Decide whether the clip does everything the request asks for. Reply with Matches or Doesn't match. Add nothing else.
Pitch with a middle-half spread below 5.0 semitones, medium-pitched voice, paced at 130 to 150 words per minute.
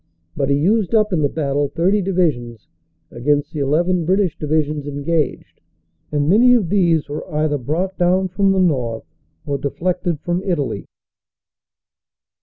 Matches